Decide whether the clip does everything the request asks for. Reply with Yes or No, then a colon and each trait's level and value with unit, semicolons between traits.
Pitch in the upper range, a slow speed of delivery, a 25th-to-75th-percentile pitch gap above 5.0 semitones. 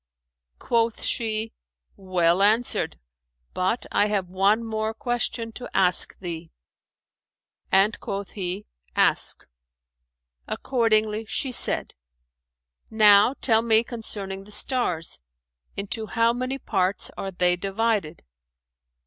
No: high, 215 Hz; slow, 105 wpm; average, 3.1 semitones